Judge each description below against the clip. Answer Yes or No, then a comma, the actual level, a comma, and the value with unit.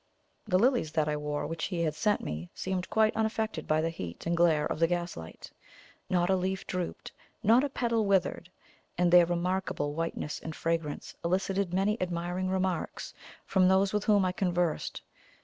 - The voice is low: No, medium, 180 Hz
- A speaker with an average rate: Yes, average, 175 wpm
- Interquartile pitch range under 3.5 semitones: Yes, average, 2.7 semitones